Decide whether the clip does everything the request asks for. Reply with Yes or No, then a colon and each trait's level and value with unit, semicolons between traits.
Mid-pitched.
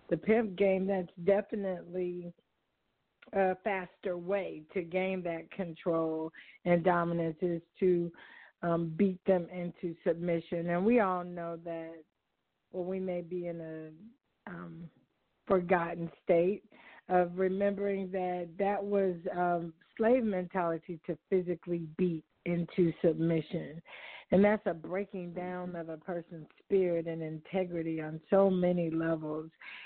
Yes: medium, 180 Hz